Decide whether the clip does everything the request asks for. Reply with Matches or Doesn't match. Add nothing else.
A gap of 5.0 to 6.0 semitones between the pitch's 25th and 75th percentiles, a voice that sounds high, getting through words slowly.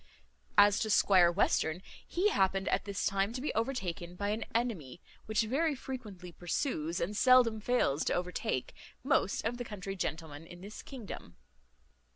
Doesn't match